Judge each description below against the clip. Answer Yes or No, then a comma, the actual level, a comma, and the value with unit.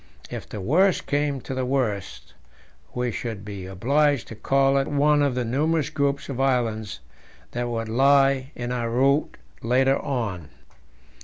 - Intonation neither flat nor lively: Yes, average, 3.4 semitones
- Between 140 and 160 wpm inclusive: Yes, average, 155 wpm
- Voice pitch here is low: Yes, low, 130 Hz